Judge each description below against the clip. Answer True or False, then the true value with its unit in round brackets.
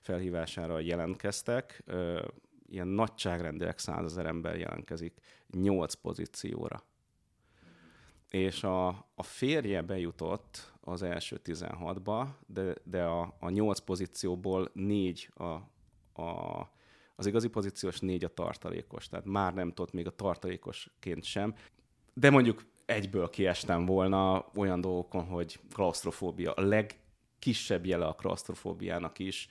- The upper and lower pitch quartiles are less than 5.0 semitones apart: True (2.7 semitones)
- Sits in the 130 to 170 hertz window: False (95 Hz)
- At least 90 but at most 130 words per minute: True (110 wpm)